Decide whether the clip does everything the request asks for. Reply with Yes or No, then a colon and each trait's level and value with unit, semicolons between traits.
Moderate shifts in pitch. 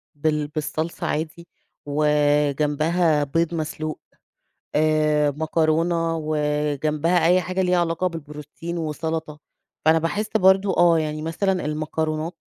No: narrow, 1.9 semitones